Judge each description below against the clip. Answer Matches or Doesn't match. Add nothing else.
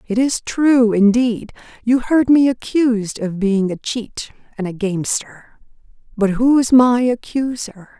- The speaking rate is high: Doesn't match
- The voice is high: Matches